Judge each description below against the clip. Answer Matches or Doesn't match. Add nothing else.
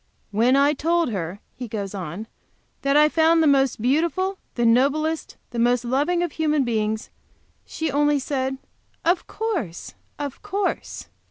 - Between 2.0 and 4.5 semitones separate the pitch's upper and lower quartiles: Doesn't match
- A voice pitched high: Matches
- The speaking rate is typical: Matches